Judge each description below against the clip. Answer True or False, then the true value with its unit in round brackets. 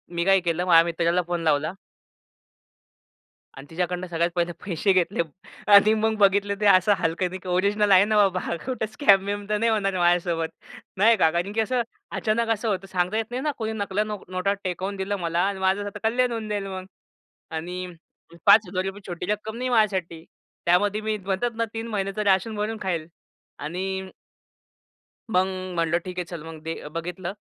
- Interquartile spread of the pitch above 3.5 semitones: False (3.1 semitones)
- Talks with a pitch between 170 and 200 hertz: True (190 Hz)